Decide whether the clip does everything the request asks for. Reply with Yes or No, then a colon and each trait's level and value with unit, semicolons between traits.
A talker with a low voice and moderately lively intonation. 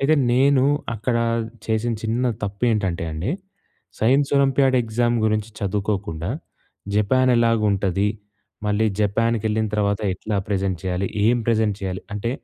Yes: low, 110 Hz; average, 3.0 semitones